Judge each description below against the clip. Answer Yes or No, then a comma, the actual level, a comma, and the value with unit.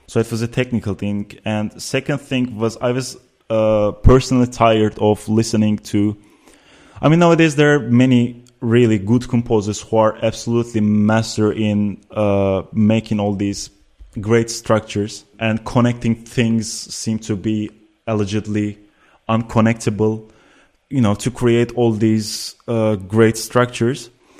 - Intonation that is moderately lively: No, narrow, 2.0 semitones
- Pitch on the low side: Yes, low, 110 Hz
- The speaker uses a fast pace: No, slow, 135 wpm